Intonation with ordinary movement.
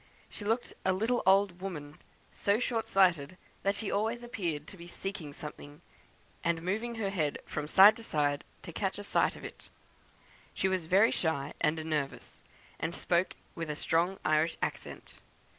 Yes: average, 4.6 semitones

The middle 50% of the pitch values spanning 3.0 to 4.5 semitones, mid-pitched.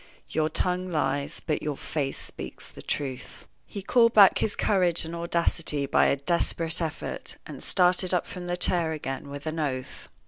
Yes: average, 3.6 semitones; medium, 165 Hz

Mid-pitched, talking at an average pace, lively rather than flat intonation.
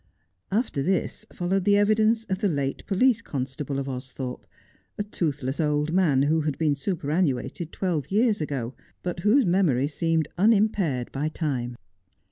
Yes: medium, 160 Hz; average, 145 wpm; wide, 6.0 semitones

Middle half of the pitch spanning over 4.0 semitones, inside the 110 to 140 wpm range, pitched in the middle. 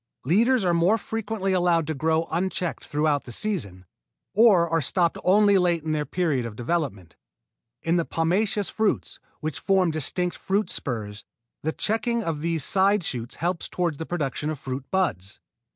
No: average, 4.4 semitones; average, 165 wpm; medium, 170 Hz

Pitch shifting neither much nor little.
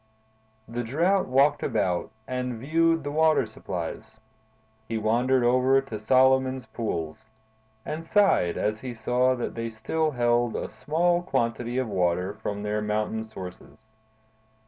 Yes: average, 3.7 semitones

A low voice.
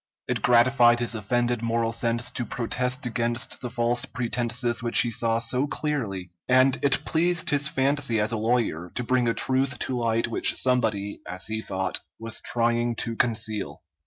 Yes: low, 120 Hz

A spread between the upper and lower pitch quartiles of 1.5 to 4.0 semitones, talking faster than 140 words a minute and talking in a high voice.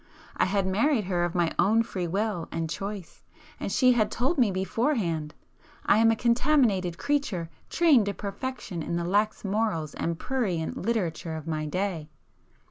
No: average, 5.1 semitones; average, 155 wpm; high, 195 Hz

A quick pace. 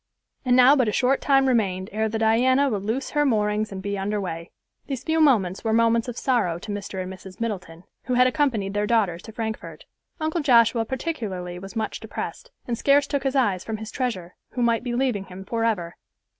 Yes: fast, 210 wpm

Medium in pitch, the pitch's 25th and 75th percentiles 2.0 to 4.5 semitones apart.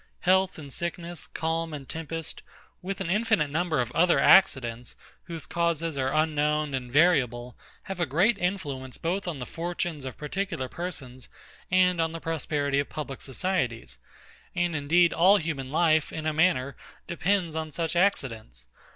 Yes: medium, 160 Hz; average, 4.0 semitones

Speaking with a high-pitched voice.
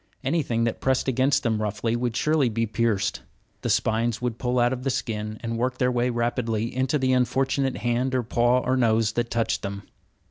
No: low, 120 Hz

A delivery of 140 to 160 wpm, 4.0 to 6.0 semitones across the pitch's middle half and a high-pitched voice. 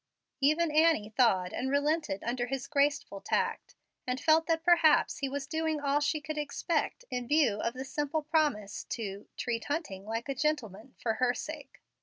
No: average, 175 wpm; average, 4.5 semitones; very high, 280 Hz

